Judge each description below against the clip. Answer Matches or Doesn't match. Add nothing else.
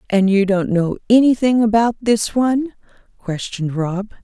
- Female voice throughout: Matches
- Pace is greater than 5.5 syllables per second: Doesn't match